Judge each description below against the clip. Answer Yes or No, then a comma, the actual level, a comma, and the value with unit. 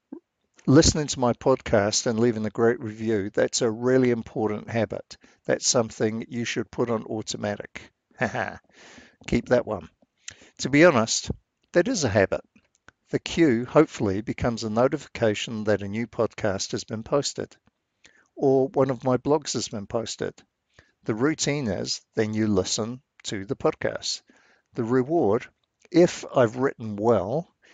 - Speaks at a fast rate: No, average, 145 wpm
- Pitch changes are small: No, average, 3.3 semitones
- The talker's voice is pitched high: No, low, 120 Hz